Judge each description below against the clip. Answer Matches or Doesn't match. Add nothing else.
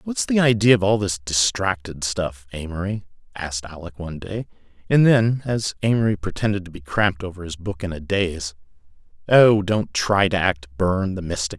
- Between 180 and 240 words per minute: Matches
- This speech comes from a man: Matches